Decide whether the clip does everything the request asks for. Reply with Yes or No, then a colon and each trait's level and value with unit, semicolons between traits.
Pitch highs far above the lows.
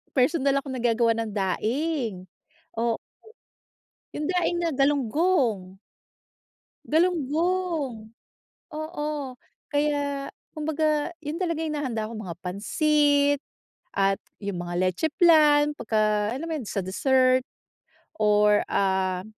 Yes: wide, 6.3 semitones